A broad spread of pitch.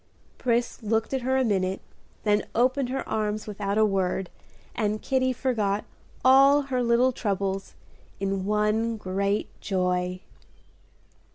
No: average, 4.1 semitones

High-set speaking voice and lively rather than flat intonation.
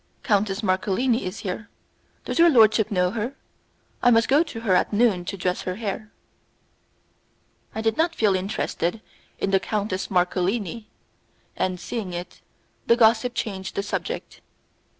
No: high, 210 Hz; average, 3.6 semitones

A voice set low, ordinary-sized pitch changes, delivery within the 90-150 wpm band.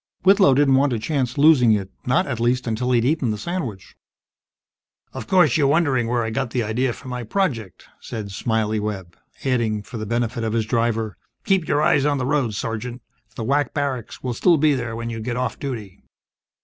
No: low, 125 Hz; average, 3.9 semitones; average, 200 wpm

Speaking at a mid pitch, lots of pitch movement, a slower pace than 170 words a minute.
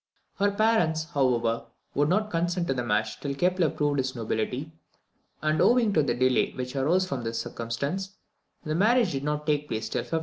No: medium, 150 Hz; wide, 6.0 semitones; average, 190 wpm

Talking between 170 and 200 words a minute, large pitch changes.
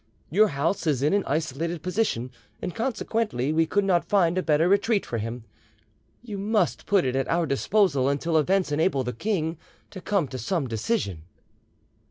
Yes: average, 175 wpm; wide, 6.3 semitones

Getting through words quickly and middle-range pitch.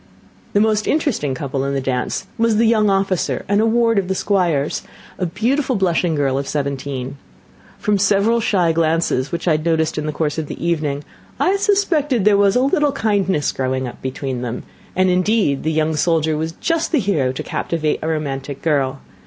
No: average, 195 wpm; medium, 170 Hz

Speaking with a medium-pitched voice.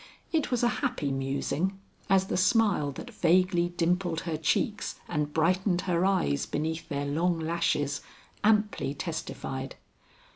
Yes: medium, 170 Hz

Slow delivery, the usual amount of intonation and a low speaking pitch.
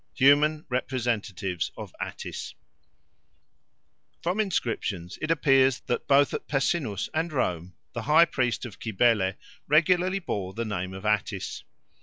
No: slow, 125 wpm; wide, 7.1 semitones; low, 125 Hz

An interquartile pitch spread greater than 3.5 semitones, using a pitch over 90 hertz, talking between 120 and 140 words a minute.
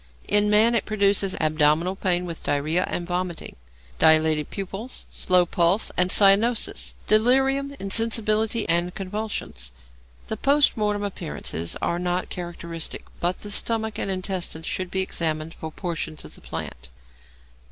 Yes: average, 4.0 semitones; medium, 185 Hz; slow, 135 wpm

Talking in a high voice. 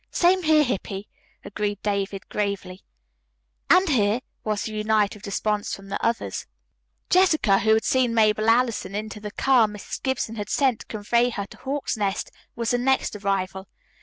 Yes: high, 215 Hz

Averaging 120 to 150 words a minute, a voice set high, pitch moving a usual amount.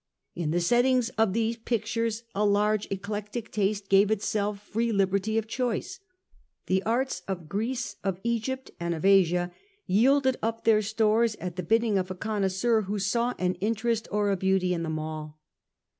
No: average, 170 wpm; high, 210 Hz; average, 3.1 semitones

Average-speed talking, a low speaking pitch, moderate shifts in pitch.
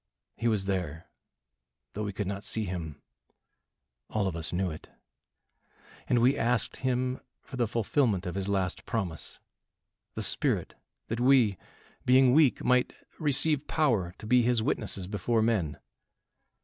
Yes: average, 145 wpm; low, 110 Hz; average, 4.8 semitones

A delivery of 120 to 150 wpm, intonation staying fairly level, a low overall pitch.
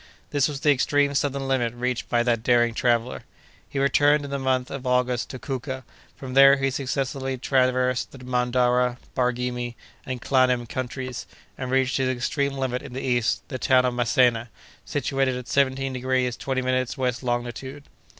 No: average, 170 wpm; narrow, 1.5 semitones; low, 130 Hz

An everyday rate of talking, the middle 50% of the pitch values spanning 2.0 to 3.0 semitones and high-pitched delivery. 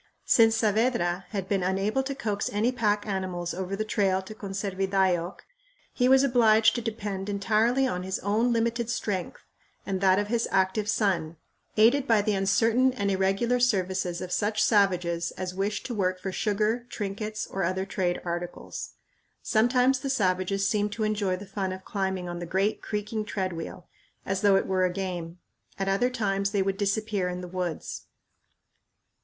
Yes: average, 170 wpm; average, 2.7 semitones; high, 200 Hz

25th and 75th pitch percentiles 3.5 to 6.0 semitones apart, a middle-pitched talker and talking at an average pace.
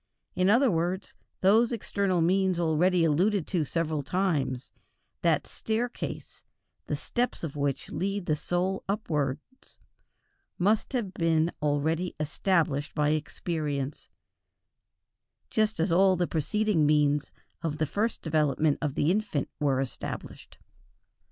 No: average, 4.5 semitones; medium, 165 Hz; slow, 120 wpm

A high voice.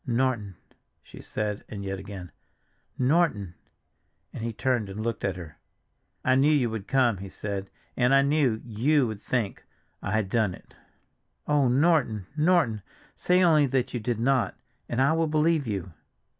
No: low, 120 Hz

